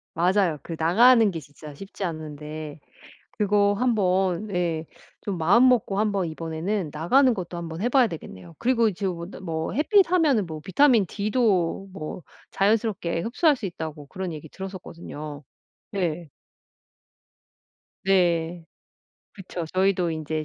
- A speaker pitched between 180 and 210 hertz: Yes, medium, 185 Hz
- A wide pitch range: No, average, 4.5 semitones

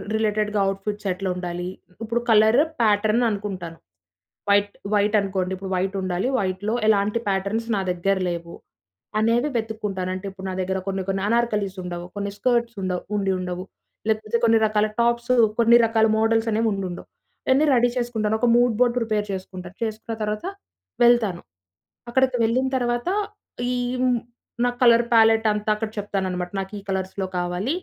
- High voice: Yes, high, 210 Hz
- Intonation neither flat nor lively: Yes, average, 3.2 semitones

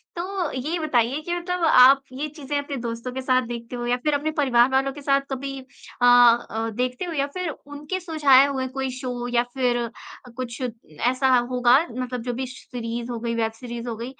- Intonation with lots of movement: No, average, 2.9 semitones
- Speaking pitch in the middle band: No, very high, 255 Hz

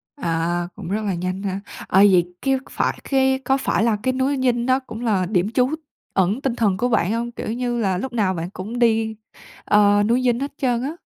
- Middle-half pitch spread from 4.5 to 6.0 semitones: Yes, average, 4.8 semitones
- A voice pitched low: No, high, 225 Hz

